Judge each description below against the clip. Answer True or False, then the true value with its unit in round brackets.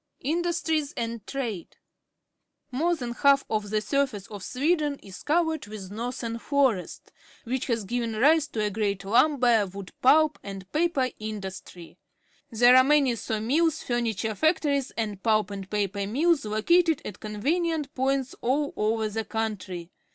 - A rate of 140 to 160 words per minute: True (150 wpm)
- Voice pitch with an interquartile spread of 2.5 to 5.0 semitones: False (5.4 semitones)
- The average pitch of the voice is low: False (235 Hz)